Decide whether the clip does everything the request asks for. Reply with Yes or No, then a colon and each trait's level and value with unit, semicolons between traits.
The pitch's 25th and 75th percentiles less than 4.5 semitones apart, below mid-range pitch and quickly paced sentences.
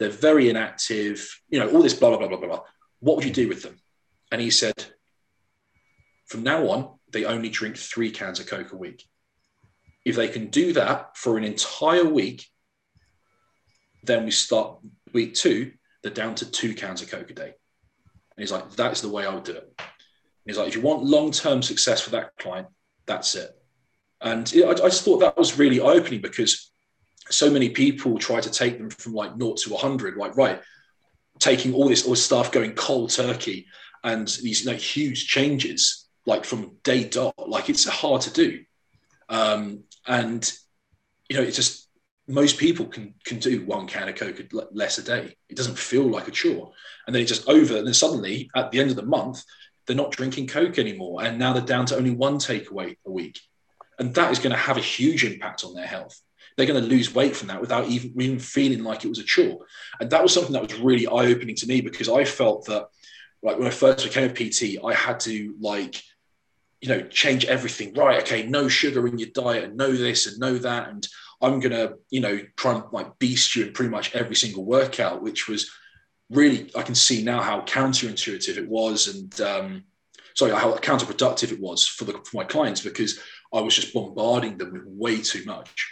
Yes: average, 4.1 semitones; low, 130 Hz; fast, 210 wpm